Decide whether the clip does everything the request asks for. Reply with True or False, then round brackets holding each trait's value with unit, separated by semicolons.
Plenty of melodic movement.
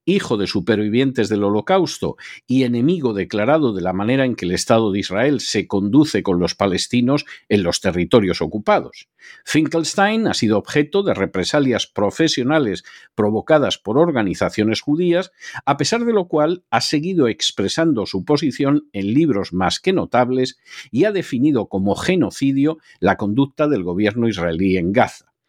True (7.2 semitones)